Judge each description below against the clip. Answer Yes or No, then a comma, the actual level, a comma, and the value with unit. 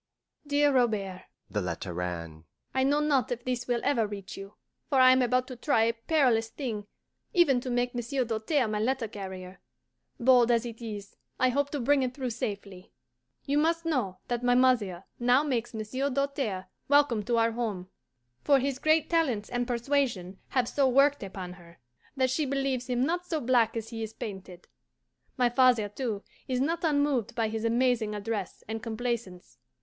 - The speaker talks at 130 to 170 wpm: No, average, 180 wpm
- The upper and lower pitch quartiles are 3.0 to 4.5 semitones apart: Yes, average, 4.0 semitones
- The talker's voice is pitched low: No, high, 240 Hz